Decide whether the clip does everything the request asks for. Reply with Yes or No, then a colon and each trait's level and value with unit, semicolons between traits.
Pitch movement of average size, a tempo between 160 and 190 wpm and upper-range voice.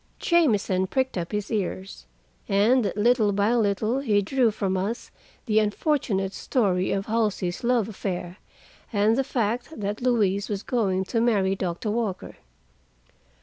No: average, 3.4 semitones; average, 140 wpm; high, 210 Hz